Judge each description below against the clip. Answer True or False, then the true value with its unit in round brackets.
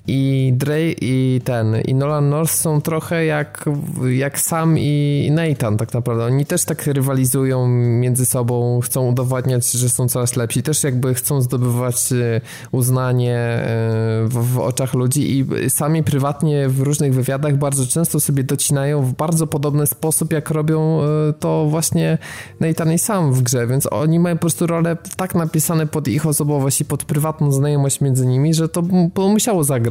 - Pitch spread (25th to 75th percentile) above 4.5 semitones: False (3.6 semitones)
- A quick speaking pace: True (165 wpm)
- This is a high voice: False (140 Hz)